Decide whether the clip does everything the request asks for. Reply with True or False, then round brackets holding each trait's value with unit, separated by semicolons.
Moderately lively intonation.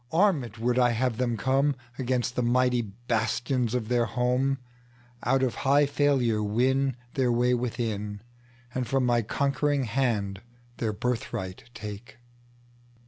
False (1.9 semitones)